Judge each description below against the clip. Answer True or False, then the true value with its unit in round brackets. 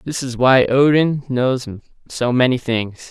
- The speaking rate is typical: True (155 wpm)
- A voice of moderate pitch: False (130 Hz)